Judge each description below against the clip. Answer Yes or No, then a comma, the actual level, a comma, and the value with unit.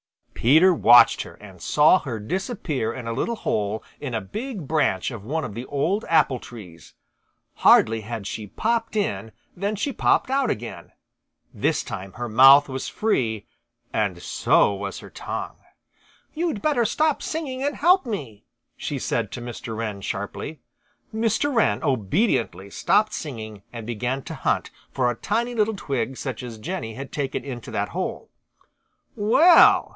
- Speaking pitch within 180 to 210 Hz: No, low, 135 Hz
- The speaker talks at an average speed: Yes, average, 160 wpm